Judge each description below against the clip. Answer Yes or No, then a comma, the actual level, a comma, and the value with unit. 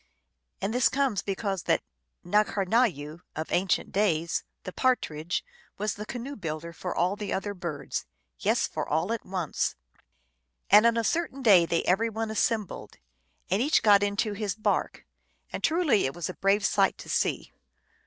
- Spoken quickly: No, average, 165 wpm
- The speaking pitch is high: Yes, high, 200 Hz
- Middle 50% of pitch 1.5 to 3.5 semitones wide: No, average, 4.3 semitones